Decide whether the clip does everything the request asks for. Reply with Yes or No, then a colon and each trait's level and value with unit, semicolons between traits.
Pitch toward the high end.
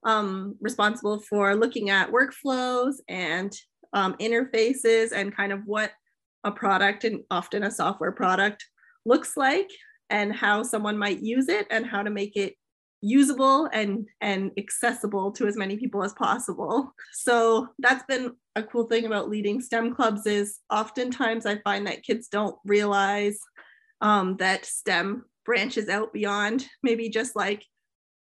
Yes: high, 215 Hz